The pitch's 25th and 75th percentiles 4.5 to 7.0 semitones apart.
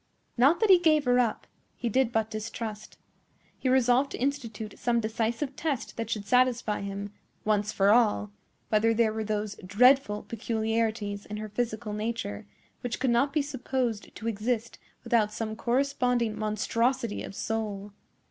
No: average, 2.8 semitones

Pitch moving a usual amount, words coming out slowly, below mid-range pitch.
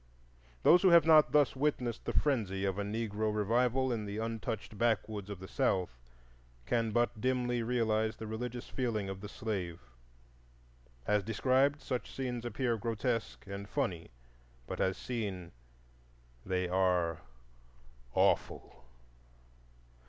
Yes: average, 3.6 semitones; slow, 130 wpm; low, 110 Hz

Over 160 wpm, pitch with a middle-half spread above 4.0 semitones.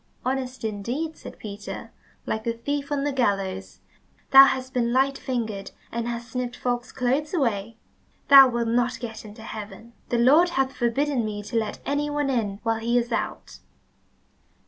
No: average, 170 wpm; average, 3.2 semitones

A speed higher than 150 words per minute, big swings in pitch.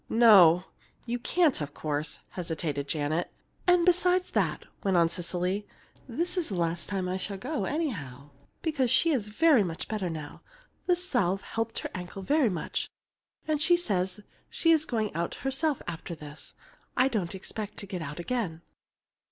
Yes: average, 160 wpm; wide, 8.4 semitones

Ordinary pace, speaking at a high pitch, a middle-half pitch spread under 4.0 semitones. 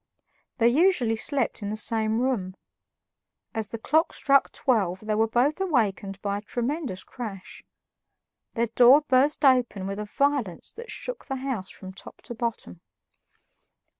No: average, 150 wpm; high, 235 Hz; average, 4.9 semitones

